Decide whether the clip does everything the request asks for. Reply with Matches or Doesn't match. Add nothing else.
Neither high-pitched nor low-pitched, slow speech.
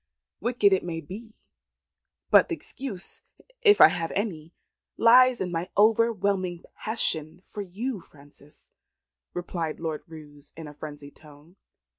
Matches